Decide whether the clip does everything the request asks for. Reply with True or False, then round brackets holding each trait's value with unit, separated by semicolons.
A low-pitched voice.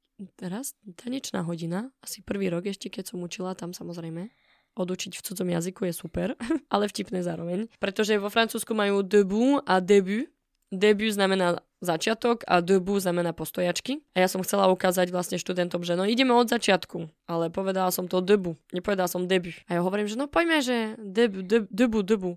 False (190 Hz)